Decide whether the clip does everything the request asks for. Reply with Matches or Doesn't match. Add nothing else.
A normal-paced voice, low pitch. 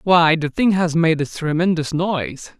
Doesn't match